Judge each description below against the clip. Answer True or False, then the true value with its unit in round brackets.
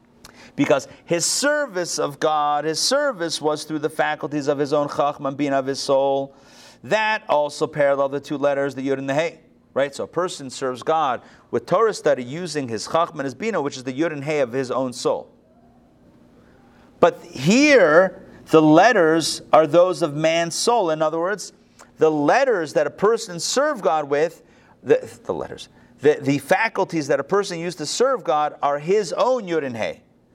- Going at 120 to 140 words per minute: False (185 wpm)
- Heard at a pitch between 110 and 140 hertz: False (155 Hz)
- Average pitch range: True (4.0 semitones)